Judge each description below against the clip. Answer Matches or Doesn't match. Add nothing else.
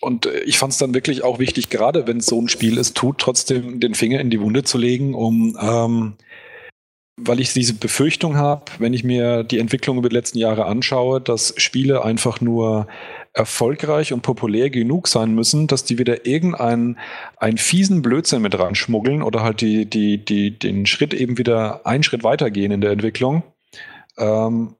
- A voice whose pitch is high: Doesn't match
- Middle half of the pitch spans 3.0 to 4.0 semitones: Doesn't match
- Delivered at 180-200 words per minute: Matches